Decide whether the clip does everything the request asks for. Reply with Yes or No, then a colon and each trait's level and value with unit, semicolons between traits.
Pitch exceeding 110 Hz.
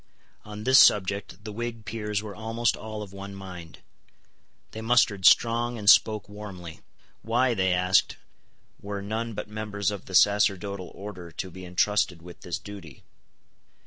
No: low, 105 Hz